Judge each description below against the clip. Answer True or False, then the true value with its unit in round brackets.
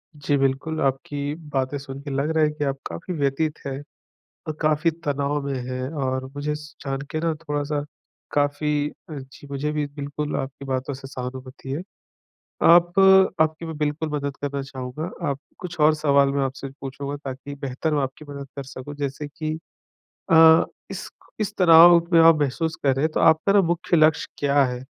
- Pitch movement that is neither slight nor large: False (2.3 semitones)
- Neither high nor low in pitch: True (145 Hz)